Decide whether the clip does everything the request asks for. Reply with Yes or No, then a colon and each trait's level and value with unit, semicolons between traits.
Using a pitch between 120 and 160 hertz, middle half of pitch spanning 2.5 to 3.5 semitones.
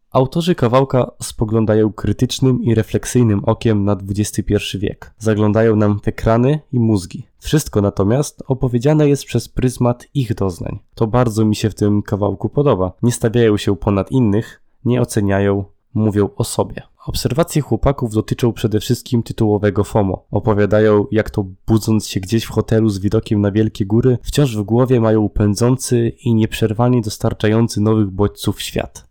No: low, 110 Hz; average, 2.8 semitones